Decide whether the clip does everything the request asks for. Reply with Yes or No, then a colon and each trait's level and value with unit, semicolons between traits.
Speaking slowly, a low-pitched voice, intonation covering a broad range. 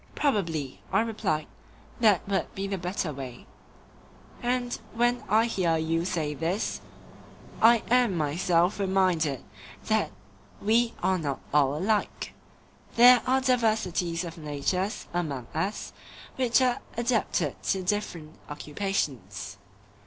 No: slow, 115 wpm; medium, 185 Hz; wide, 6.1 semitones